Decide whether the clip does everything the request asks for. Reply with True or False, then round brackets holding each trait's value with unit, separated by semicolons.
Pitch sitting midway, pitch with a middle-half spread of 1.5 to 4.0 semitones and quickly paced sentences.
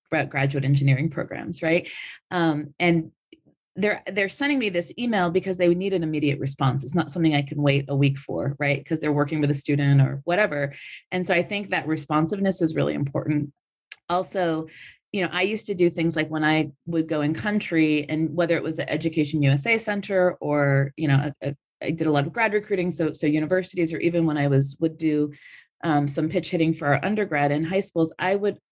True (160 Hz; 3.5 semitones; 215 wpm)